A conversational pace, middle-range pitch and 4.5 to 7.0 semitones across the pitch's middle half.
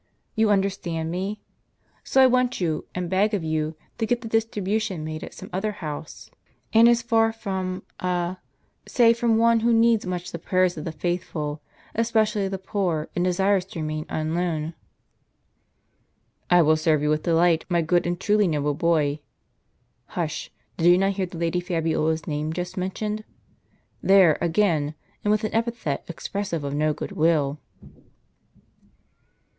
Yes: average, 160 wpm; medium, 180 Hz; average, 4.8 semitones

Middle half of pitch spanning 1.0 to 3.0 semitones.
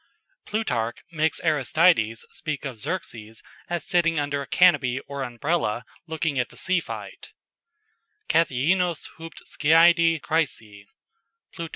No: average, 5.1 semitones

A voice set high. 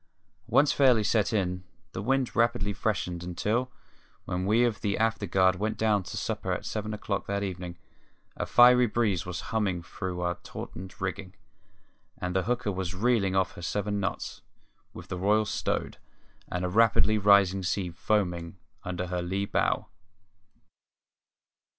No: low, 100 Hz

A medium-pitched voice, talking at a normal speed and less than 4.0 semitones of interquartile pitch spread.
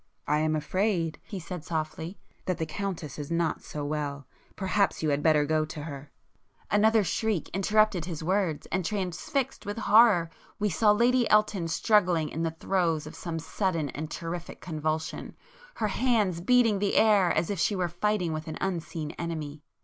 No: medium, 170 Hz; average, 165 wpm; average, 4.7 semitones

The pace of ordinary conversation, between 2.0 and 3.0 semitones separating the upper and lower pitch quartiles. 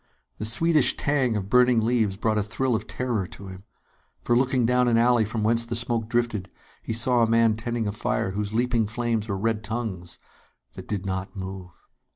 Yes: average, 195 wpm; average, 2.7 semitones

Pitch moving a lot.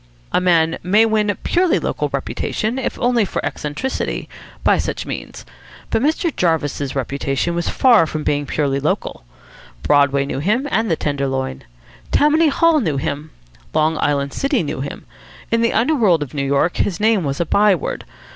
Yes: wide, 8.0 semitones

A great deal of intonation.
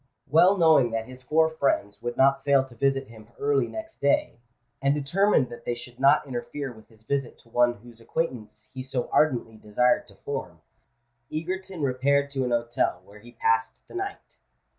No: average, 3.2 semitones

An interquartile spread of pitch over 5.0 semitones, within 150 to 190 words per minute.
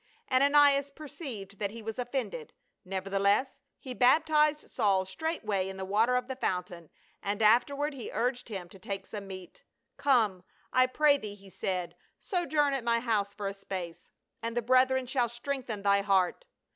Yes: wide, 5.4 semitones; average, 175 wpm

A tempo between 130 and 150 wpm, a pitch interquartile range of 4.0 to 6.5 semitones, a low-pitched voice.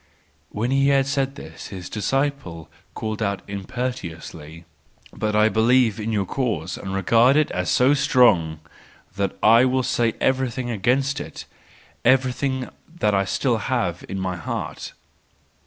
Yes: average, 140 wpm; average, 5.2 semitones; low, 115 Hz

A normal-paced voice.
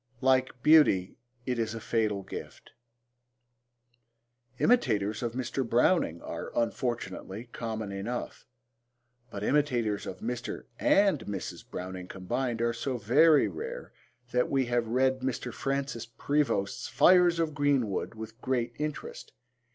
No: slow, 125 wpm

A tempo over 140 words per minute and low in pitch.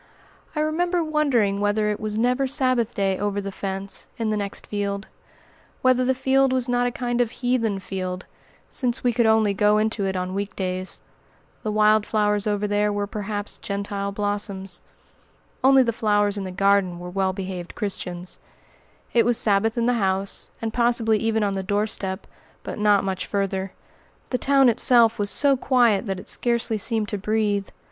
No: average, 180 wpm; high, 210 Hz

